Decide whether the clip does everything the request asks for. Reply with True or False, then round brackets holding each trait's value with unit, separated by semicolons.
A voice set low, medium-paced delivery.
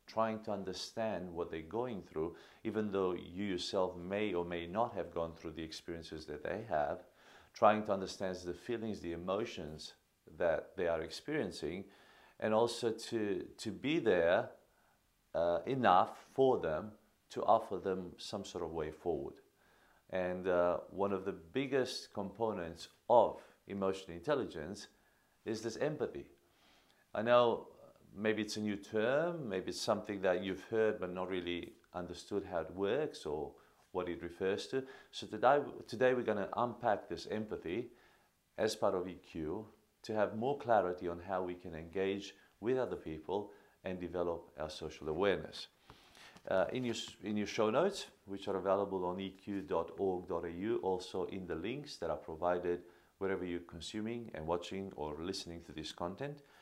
True (95 Hz; 160 wpm)